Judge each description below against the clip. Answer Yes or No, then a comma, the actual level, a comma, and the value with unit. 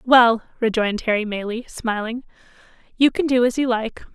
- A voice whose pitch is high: Yes, high, 235 Hz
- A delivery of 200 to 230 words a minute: No, average, 160 wpm